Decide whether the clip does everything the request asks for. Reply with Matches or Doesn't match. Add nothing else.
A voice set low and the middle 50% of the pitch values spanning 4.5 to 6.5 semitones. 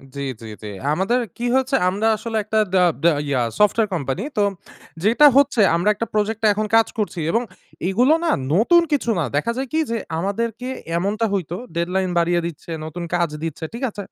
Doesn't match